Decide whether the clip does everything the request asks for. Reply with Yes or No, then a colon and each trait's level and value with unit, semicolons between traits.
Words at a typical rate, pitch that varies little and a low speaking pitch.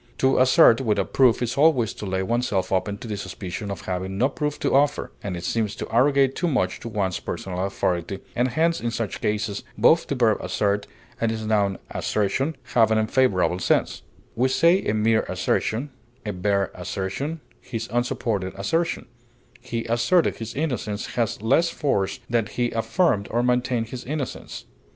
No: average, 170 wpm; average, 4.5 semitones; low, 115 Hz